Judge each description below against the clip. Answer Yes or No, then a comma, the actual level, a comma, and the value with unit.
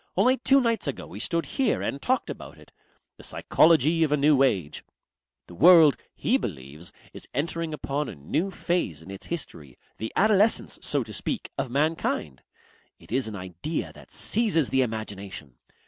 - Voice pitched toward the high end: No, medium, 140 Hz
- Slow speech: No, average, 170 wpm